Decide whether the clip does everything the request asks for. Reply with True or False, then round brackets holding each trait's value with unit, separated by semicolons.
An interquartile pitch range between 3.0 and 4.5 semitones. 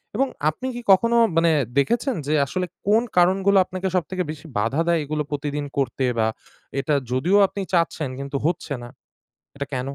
False (5.2 semitones)